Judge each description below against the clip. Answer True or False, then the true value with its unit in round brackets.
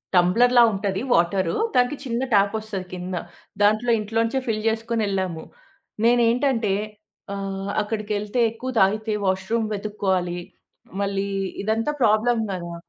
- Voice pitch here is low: False (210 Hz)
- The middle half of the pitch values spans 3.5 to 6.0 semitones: False (2.9 semitones)